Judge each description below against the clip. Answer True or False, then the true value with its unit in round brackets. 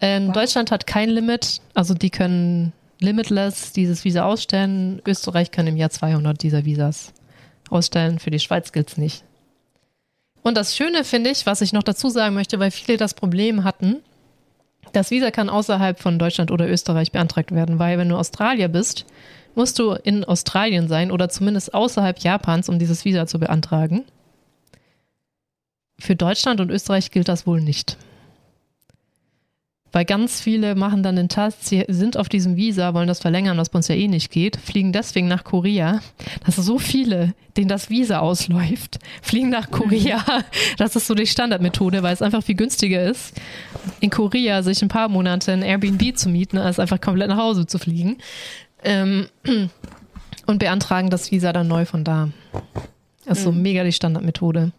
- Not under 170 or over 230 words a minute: True (175 wpm)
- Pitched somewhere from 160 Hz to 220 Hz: True (190 Hz)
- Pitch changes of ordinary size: True (3.2 semitones)